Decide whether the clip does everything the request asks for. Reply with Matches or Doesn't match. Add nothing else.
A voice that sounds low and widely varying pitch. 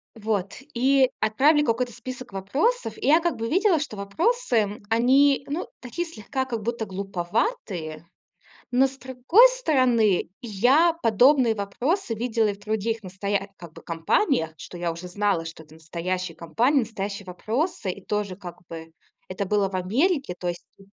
Doesn't match